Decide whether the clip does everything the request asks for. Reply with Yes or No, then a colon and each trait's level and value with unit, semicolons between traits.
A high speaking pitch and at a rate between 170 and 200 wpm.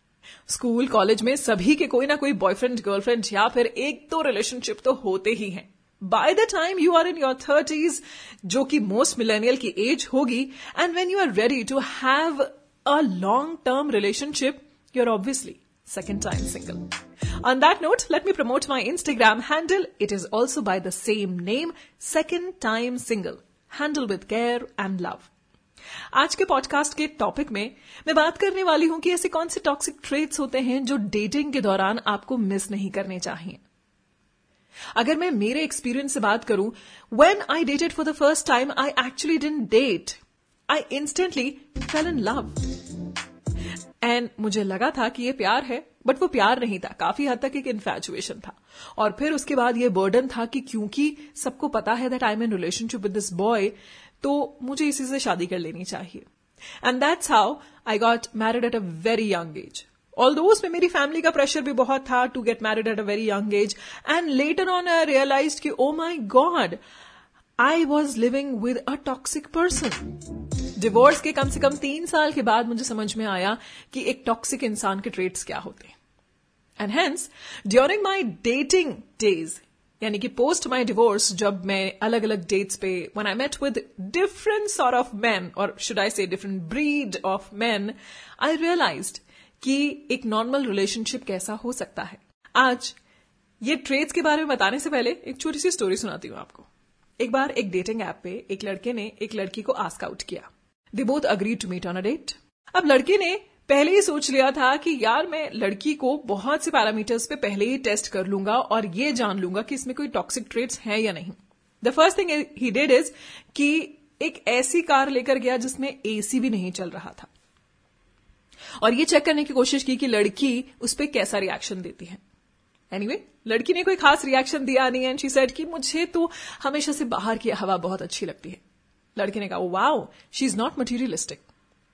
Yes: very high, 255 Hz; average, 185 wpm